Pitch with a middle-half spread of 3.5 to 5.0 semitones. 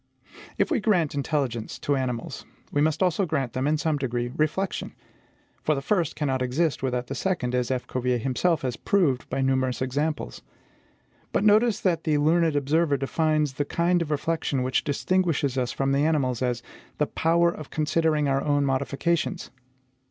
Yes: average, 3.9 semitones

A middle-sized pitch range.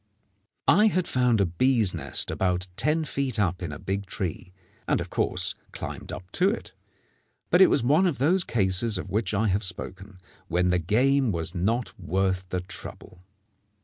No: wide, 6.2 semitones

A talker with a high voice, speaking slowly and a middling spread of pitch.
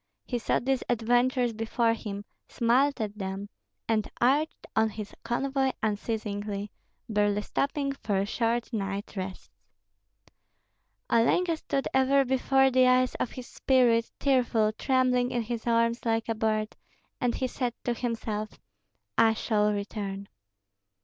Yes: high, 230 Hz; slow, 130 wpm; average, 3.1 semitones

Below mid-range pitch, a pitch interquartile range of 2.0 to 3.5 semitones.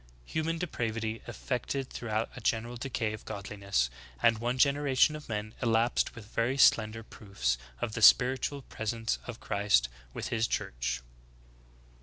Yes: low, 115 Hz; average, 2.9 semitones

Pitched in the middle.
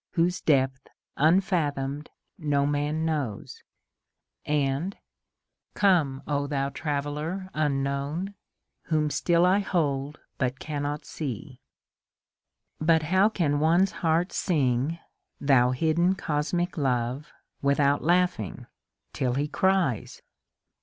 Yes: medium, 150 Hz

